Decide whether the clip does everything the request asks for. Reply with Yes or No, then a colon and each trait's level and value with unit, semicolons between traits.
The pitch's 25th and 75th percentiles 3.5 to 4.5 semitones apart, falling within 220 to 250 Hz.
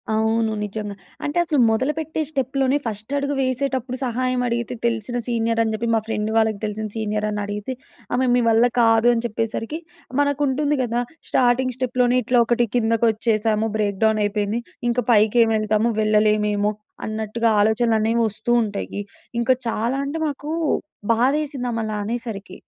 No: average, 2.8 semitones; high, 230 Hz